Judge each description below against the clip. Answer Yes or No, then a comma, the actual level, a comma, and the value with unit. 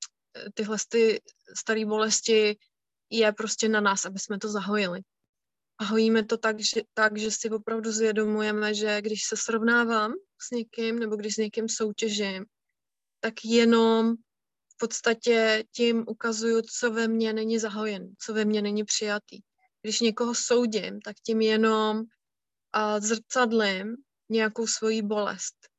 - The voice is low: No, high, 220 Hz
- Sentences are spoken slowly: No, average, 135 wpm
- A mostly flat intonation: Yes, narrow, 1.2 semitones